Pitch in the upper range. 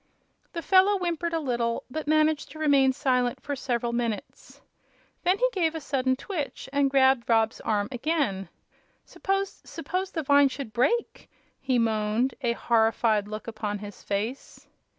Yes: very high, 265 Hz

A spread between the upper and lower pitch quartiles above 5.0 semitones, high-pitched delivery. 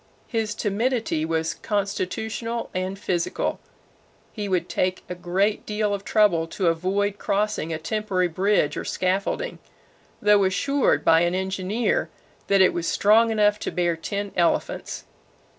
No: average, 2.8 semitones; high, 195 Hz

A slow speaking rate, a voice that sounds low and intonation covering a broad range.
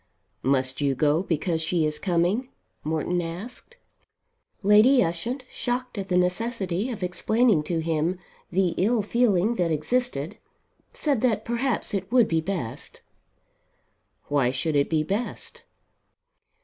No: slow, 130 wpm; medium, 185 Hz; wide, 6.5 semitones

